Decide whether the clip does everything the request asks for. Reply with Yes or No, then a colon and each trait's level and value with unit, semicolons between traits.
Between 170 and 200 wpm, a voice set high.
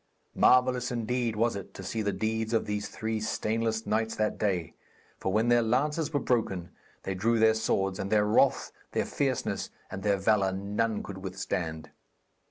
No: average, 175 wpm; low, 110 Hz